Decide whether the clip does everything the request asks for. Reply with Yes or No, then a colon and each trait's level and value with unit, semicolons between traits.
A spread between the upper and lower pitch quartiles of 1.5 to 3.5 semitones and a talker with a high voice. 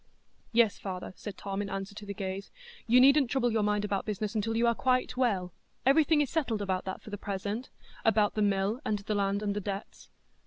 Yes: average, 2.9 semitones; high, 210 Hz